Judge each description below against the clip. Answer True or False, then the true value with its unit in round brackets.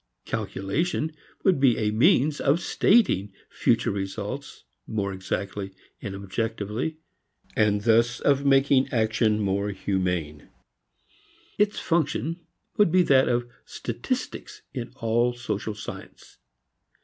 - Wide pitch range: True (5.7 semitones)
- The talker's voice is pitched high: False (115 Hz)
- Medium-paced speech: False (110 wpm)